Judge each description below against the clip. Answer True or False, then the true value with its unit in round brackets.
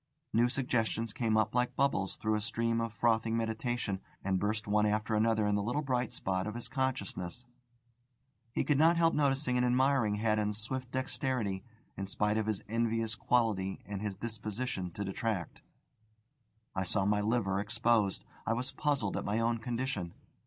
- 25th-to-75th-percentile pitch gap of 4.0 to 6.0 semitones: False (3.0 semitones)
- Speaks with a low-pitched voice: True (110 Hz)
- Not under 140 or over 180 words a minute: True (170 wpm)